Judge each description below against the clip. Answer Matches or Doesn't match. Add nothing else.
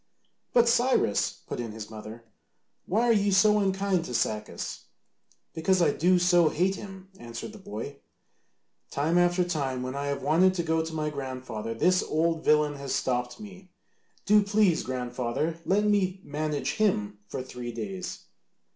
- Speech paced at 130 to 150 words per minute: Doesn't match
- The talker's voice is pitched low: Doesn't match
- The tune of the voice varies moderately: Doesn't match